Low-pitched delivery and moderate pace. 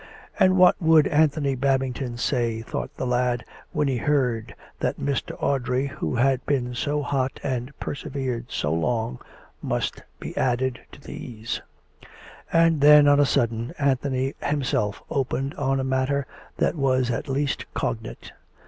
Yes: low, 130 Hz; average, 150 wpm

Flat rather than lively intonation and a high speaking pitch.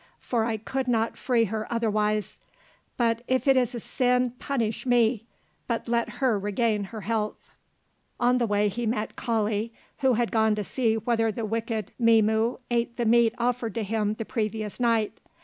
Yes: narrow, 1.9 semitones; high, 230 Hz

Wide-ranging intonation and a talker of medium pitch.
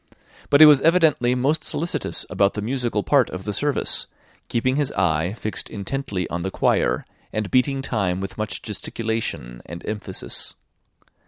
No: wide, 5.8 semitones; low, 110 Hz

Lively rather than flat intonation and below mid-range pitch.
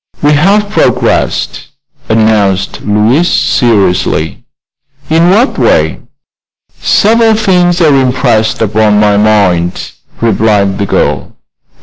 Yes: wide, 8.8 semitones; low, 110 Hz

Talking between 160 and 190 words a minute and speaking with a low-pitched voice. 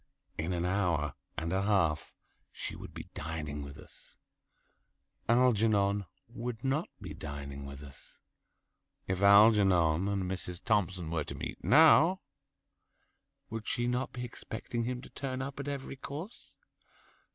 No: average, 140 wpm; low, 100 Hz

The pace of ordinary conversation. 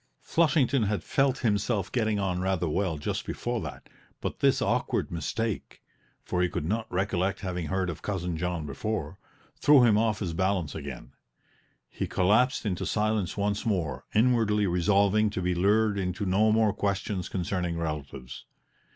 Yes: average, 155 wpm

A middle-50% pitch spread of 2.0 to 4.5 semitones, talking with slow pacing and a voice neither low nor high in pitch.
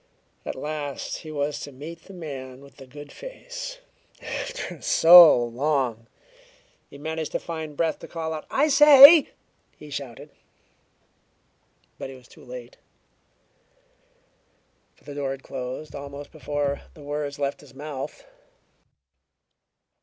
Yes: average, 2.9 semitones; slow, 130 wpm; medium, 145 Hz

